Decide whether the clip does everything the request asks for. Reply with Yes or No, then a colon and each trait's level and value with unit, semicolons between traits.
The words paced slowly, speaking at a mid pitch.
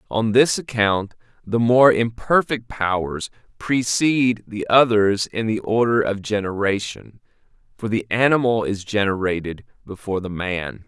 No: slow, 125 wpm; low, 110 Hz